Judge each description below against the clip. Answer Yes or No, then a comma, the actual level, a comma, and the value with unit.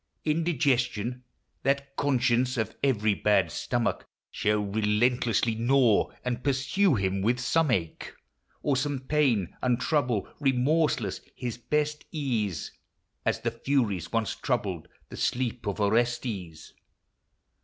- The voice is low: Yes, low, 120 Hz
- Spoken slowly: Yes, slow, 115 wpm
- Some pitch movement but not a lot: Yes, average, 4.6 semitones